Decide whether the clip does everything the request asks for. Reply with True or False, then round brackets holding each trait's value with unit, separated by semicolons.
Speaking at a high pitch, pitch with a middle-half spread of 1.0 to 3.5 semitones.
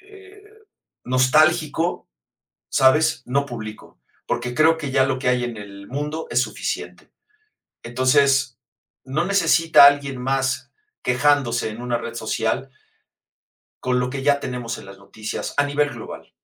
False (130 Hz; 3.1 semitones)